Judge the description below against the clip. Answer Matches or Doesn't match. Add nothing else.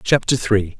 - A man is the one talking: Matches